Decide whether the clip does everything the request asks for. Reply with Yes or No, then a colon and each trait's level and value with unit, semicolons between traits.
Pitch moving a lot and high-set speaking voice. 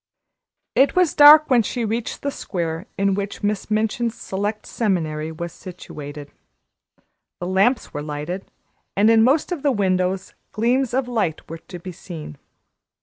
Yes: wide, 5.7 semitones; high, 200 Hz